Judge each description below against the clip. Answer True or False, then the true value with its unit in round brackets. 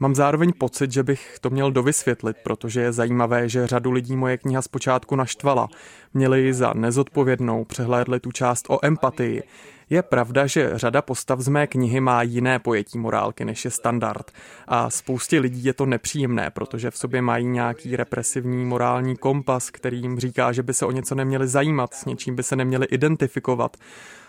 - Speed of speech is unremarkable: False (180 wpm)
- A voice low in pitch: True (130 Hz)